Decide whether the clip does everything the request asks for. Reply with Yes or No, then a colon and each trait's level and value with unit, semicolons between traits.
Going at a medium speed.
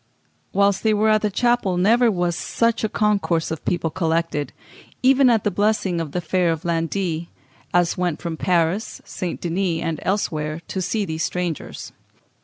Yes: average, 170 wpm